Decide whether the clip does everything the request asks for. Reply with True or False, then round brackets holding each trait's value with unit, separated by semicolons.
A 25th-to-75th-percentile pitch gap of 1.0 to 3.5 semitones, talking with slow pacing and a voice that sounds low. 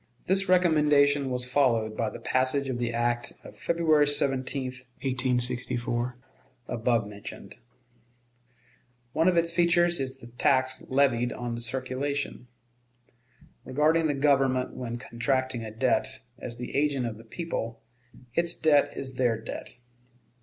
True (3.2 semitones; 130 wpm; 130 Hz)